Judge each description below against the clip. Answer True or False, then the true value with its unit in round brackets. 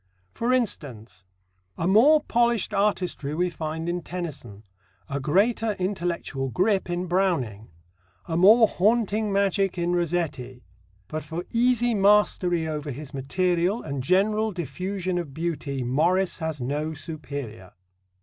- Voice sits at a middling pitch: True (175 Hz)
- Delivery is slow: True (125 wpm)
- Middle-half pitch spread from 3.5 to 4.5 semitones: False (5.3 semitones)